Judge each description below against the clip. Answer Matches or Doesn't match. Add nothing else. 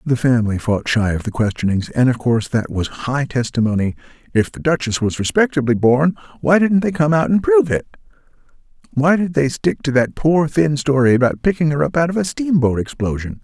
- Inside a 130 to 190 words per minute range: Doesn't match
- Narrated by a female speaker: Doesn't match